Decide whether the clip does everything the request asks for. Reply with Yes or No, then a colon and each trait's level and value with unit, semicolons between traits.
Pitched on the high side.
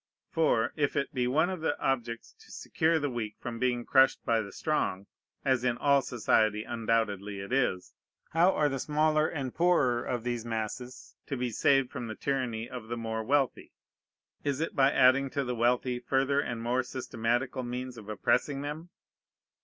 No: low, 125 Hz